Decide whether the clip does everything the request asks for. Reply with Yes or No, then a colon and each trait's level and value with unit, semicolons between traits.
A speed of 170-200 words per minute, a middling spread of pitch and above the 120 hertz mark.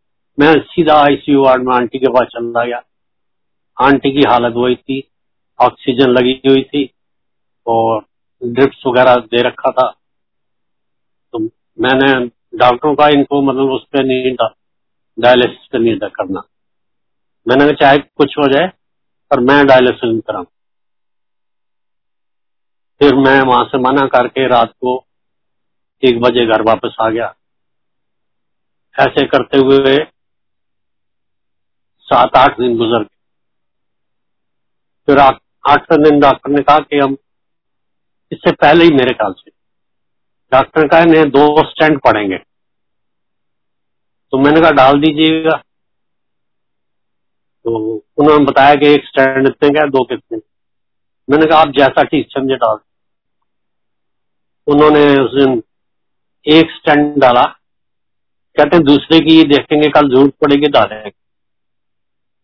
No: average, 120 wpm; average, 3.2 semitones; low, 135 Hz